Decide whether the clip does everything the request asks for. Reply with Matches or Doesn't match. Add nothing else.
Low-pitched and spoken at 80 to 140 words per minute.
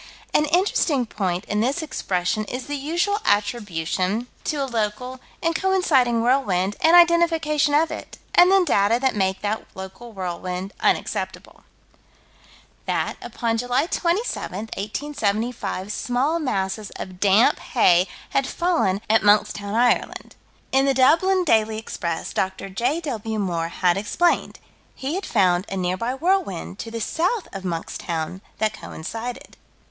Doesn't match